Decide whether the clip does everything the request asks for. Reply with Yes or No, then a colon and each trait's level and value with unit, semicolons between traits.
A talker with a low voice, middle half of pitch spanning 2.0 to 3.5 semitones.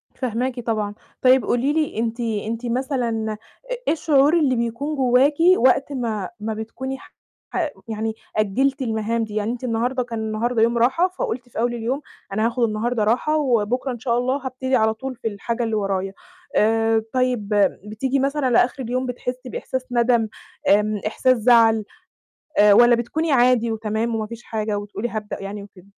No: high, 235 Hz; average, 2.7 semitones